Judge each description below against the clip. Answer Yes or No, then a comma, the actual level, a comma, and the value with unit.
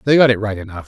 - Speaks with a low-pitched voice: Yes, low, 110 Hz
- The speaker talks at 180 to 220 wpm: No, fast, 345 wpm